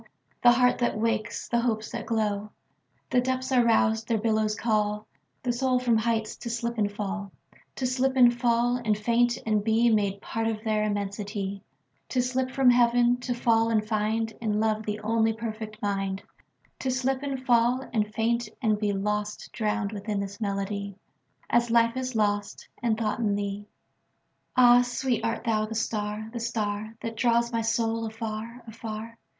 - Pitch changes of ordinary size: No, narrow, 2.1 semitones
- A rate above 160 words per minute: No, average, 150 wpm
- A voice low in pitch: No, high, 225 Hz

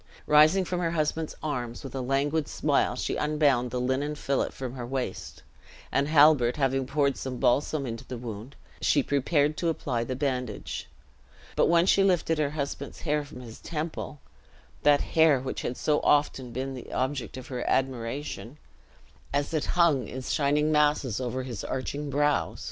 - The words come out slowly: No, average, 170 wpm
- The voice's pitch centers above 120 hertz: Yes, medium, 140 Hz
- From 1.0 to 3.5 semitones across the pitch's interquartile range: Yes, average, 2.8 semitones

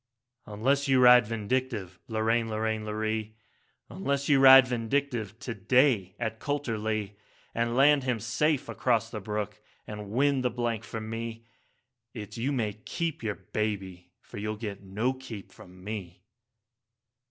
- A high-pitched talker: No, low, 115 Hz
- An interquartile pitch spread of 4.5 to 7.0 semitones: No, average, 3.4 semitones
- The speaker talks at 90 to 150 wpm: Yes, average, 145 wpm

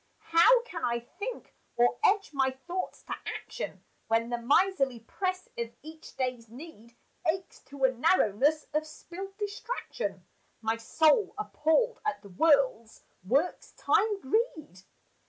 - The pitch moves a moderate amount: No, wide, 7.9 semitones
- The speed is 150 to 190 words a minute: No, slow, 135 wpm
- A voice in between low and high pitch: No, very high, 305 Hz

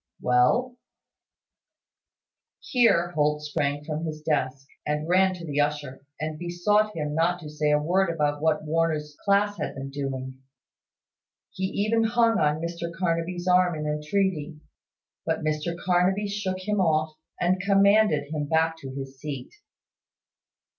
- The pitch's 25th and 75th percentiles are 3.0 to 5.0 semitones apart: Yes, average, 3.8 semitones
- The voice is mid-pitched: Yes, medium, 160 Hz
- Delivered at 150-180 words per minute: No, average, 140 wpm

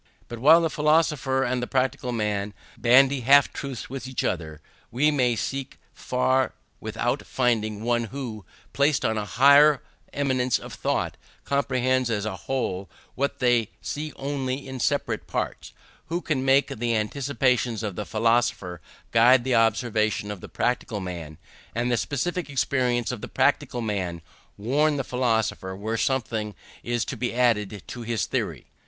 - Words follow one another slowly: No, average, 155 wpm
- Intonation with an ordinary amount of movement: Yes, average, 3.6 semitones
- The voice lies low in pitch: Yes, low, 125 Hz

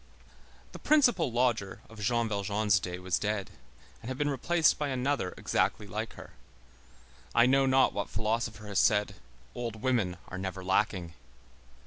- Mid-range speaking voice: No, low, 110 Hz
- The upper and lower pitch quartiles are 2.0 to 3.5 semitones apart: No, average, 4.6 semitones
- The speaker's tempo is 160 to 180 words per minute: No, average, 150 wpm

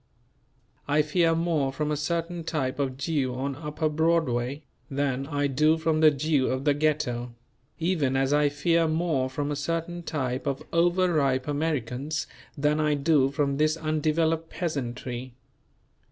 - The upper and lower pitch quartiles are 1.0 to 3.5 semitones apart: Yes, average, 3.0 semitones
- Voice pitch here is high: No, medium, 150 Hz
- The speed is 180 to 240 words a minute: No, average, 155 wpm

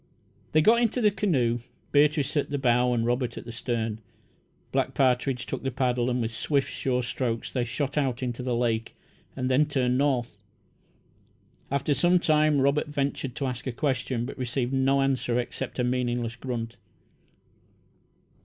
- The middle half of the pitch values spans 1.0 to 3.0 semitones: Yes, narrow, 2.5 semitones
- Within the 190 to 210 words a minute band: No, average, 165 wpm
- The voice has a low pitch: Yes, low, 130 Hz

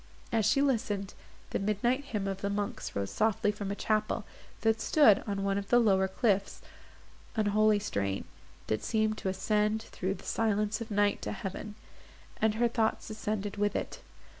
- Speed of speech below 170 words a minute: No, average, 175 wpm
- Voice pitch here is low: No, high, 210 Hz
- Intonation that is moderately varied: No, narrow, 1.8 semitones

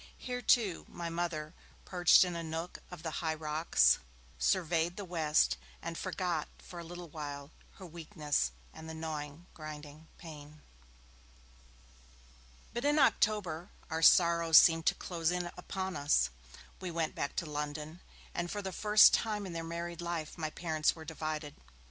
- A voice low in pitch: No, medium, 165 Hz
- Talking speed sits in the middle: Yes, average, 155 wpm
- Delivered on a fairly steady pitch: Yes, narrow, 2.3 semitones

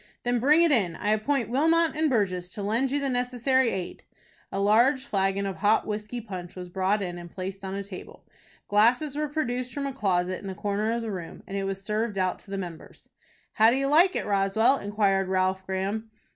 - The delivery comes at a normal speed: No, fast, 215 wpm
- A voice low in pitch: No, high, 210 Hz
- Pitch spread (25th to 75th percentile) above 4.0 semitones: Yes, average, 4.6 semitones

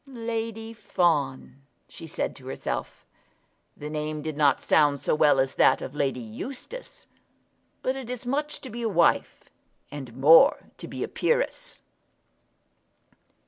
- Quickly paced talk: No, average, 140 wpm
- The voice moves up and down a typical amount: No, wide, 8.8 semitones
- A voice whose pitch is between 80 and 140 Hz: No, medium, 160 Hz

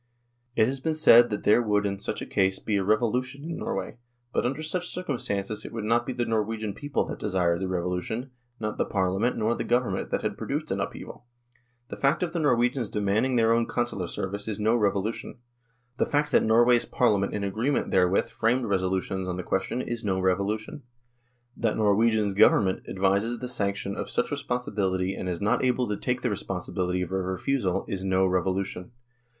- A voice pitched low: Yes, low, 105 Hz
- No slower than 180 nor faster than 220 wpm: Yes, average, 195 wpm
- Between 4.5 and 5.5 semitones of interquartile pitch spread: No, average, 4.1 semitones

